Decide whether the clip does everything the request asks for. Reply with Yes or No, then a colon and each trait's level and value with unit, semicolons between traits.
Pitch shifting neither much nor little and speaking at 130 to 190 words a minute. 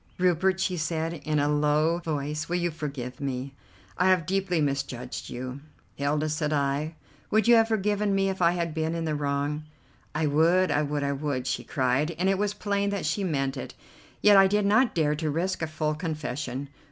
No: average, 4.3 semitones; average, 200 wpm